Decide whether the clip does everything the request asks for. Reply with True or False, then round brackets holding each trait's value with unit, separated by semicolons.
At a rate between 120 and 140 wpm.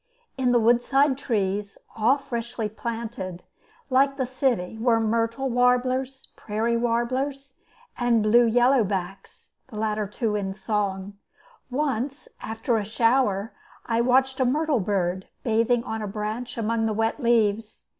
True (135 wpm)